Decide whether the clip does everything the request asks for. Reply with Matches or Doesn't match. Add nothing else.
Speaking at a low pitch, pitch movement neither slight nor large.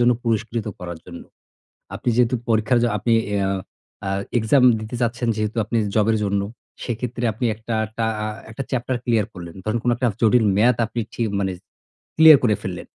Doesn't match